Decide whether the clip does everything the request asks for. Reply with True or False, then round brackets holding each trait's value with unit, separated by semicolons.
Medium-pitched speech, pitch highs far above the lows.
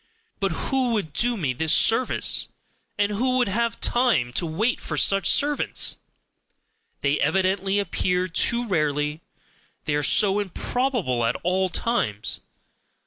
False (195 Hz; 7.2 semitones)